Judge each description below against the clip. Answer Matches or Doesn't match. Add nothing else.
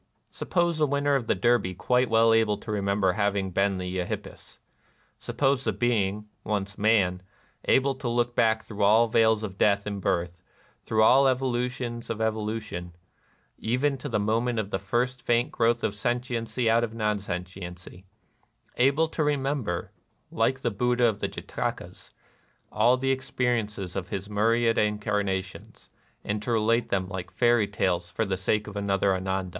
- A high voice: Doesn't match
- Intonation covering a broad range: Doesn't match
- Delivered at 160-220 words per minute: Matches